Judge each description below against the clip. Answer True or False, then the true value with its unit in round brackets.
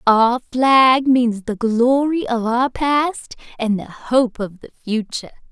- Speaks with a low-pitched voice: False (240 Hz)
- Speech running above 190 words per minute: False (150 wpm)